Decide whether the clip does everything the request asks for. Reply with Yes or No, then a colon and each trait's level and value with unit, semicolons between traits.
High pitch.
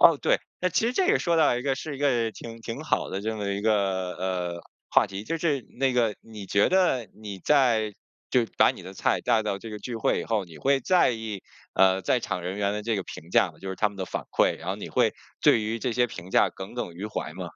No: low, 110 Hz